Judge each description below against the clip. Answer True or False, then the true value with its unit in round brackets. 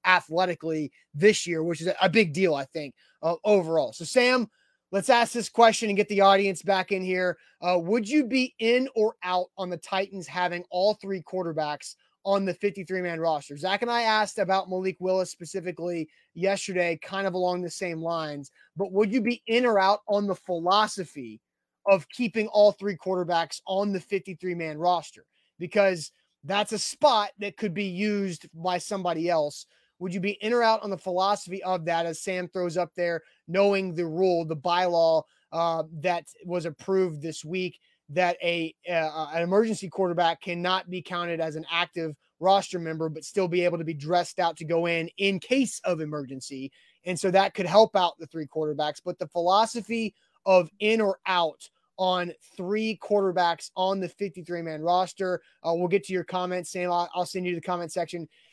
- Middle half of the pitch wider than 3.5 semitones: False (2.7 semitones)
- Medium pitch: True (180 Hz)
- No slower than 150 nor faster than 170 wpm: False (190 wpm)